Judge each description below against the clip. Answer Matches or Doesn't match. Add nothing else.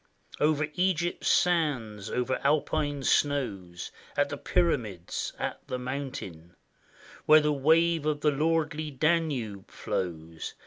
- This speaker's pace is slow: Matches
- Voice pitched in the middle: Matches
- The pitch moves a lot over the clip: Matches